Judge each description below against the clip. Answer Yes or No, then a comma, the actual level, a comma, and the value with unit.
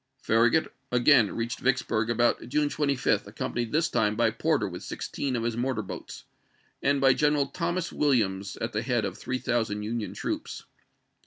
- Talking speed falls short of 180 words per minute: Yes, average, 165 wpm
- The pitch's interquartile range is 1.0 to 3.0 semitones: No, average, 3.9 semitones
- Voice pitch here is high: No, low, 120 Hz